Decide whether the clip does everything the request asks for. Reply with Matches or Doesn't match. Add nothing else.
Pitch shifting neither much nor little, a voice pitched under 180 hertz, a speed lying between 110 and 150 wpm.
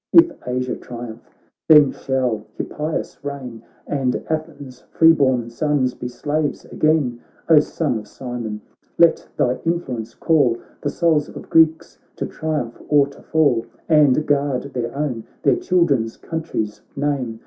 Matches